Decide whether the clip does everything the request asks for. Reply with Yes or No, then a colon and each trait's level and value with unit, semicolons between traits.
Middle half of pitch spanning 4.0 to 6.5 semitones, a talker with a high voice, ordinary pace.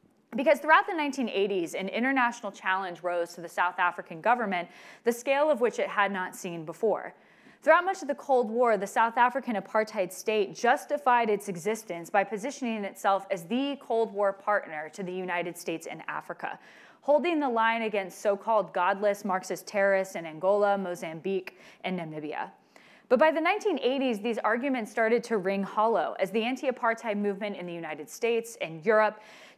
Yes: average, 4.3 semitones; high, 215 Hz; average, 170 wpm